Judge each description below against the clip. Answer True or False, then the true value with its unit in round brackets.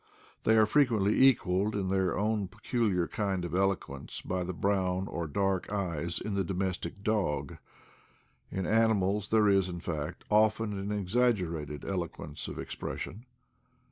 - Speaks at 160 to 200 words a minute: False (150 wpm)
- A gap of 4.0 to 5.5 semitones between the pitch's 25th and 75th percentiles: False (2.9 semitones)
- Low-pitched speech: True (95 Hz)